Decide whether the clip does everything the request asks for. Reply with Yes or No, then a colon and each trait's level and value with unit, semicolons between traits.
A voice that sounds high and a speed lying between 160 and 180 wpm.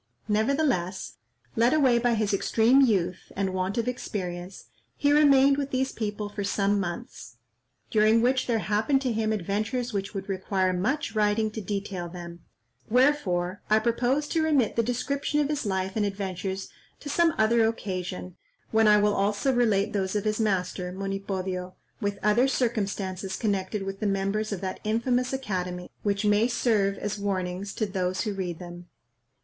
Yes: high, 210 Hz; average, 165 wpm